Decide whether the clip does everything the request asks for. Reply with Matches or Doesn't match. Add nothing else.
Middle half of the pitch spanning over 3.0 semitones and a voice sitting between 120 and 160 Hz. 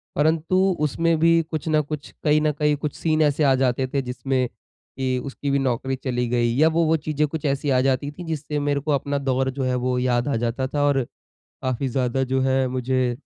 Doesn't match